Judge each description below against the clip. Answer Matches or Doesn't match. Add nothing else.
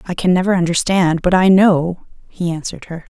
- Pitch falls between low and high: Matches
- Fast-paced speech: Doesn't match